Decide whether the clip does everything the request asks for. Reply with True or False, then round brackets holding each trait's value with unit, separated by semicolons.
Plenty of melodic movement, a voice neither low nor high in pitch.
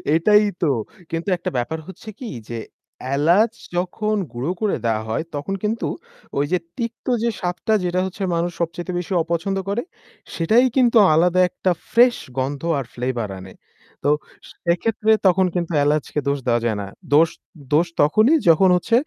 True (6.1 semitones; 175 Hz)